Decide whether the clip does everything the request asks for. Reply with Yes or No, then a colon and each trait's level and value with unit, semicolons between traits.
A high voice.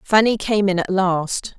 Yes: high, 195 Hz